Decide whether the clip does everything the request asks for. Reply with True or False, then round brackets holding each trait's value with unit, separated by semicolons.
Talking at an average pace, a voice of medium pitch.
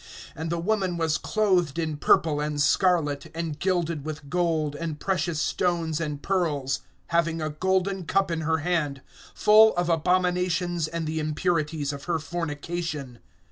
True (150 wpm; 165 Hz)